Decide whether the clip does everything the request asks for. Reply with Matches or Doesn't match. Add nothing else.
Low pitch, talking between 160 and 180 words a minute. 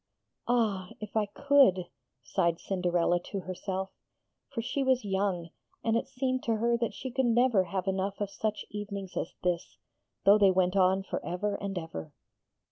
Doesn't match